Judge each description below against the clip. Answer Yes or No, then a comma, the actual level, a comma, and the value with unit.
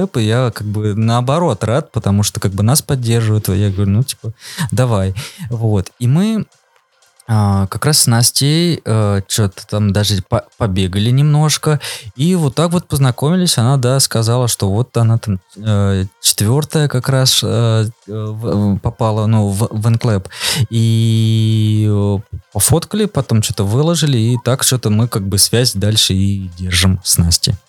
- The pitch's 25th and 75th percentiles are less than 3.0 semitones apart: No, average, 4.1 semitones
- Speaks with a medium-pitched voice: No, low, 115 Hz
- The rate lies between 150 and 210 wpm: Yes, average, 155 wpm